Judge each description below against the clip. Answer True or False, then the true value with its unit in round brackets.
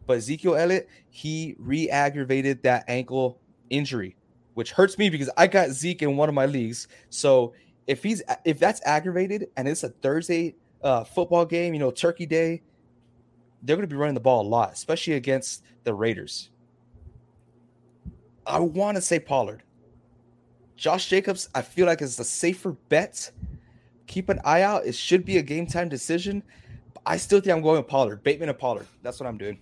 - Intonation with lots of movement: True (6.1 semitones)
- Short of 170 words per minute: False (180 wpm)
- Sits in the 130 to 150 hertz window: True (140 Hz)